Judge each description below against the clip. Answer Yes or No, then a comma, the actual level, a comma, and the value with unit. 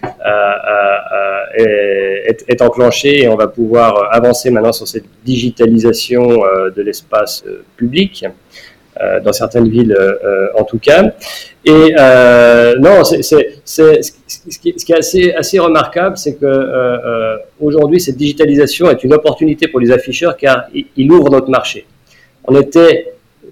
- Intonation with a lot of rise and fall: Yes, wide, 6.6 semitones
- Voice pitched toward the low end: Yes, low, 130 Hz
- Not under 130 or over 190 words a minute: Yes, average, 160 wpm